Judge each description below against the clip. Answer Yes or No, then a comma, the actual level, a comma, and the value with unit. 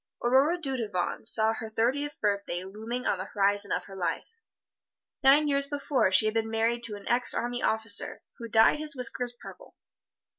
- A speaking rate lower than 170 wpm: No, average, 175 wpm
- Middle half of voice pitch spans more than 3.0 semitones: Yes, average, 4.3 semitones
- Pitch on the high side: Yes, high, 230 Hz